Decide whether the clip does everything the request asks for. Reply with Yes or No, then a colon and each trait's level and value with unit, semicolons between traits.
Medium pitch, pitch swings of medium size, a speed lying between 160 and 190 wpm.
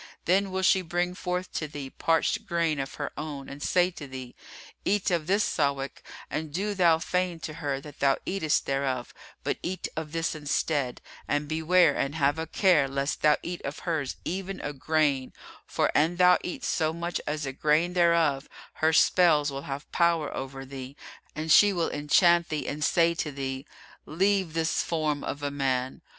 Yes: medium, 155 Hz; average, 3.6 semitones; average, 185 wpm